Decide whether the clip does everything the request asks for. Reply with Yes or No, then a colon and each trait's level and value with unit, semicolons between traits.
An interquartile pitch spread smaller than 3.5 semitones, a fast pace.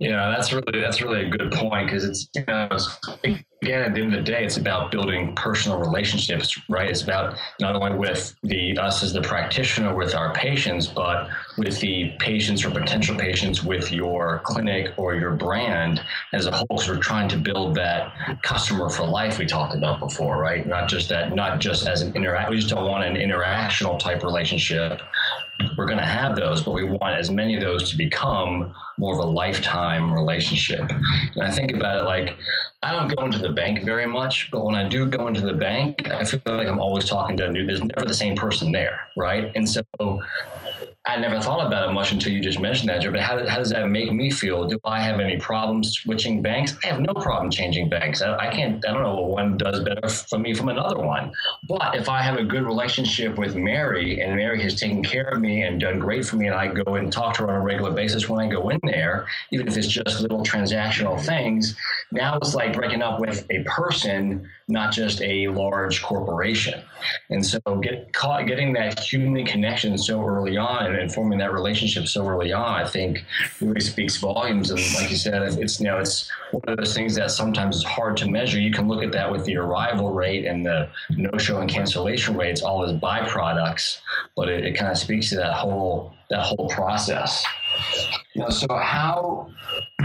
Yes: average, 2.8 semitones; fast, 215 wpm